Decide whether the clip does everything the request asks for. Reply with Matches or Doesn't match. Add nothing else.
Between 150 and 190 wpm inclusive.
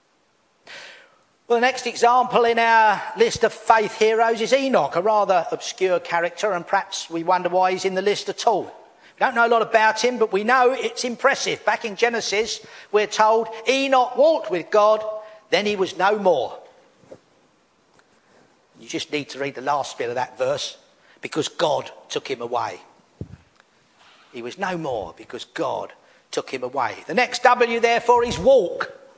Matches